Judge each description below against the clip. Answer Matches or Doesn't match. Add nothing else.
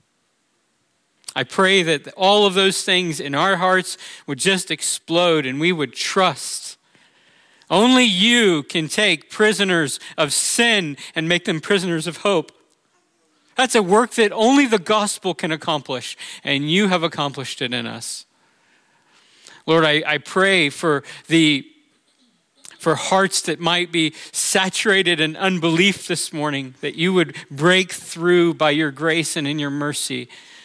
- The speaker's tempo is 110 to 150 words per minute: Matches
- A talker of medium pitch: Matches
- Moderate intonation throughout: Matches